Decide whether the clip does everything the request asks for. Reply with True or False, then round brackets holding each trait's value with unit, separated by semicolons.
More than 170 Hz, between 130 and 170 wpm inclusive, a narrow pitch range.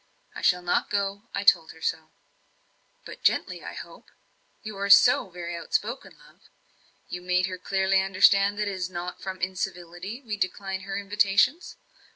True (190 Hz; 165 wpm; 2.0 semitones)